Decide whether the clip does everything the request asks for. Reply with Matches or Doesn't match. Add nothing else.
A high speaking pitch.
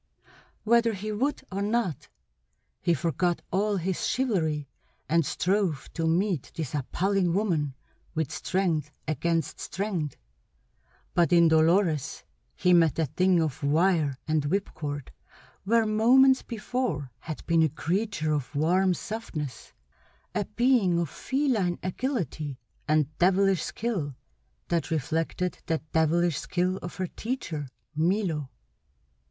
Doesn't match